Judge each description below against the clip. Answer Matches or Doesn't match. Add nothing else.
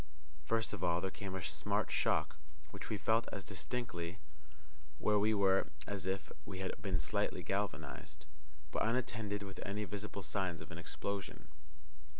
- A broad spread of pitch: Doesn't match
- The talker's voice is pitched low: Matches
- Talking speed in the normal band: Matches